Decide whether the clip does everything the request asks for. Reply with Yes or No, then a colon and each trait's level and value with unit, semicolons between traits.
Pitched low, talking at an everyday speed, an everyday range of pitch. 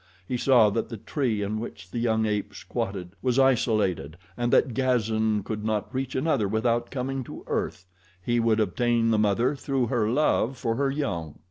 Yes: low, 115 Hz; average, 180 wpm; average, 3.2 semitones